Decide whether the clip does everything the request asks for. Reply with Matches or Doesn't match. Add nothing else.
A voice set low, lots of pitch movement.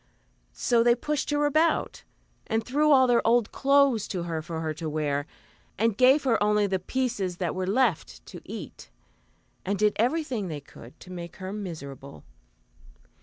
Doesn't match